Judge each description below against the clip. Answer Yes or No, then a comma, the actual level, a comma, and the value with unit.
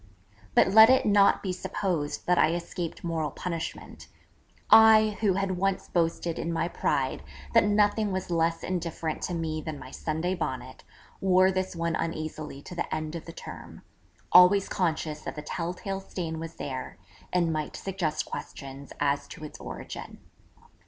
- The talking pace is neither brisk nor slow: Yes, average, 165 wpm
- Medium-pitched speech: Yes, medium, 170 Hz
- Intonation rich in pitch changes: No, average, 3.2 semitones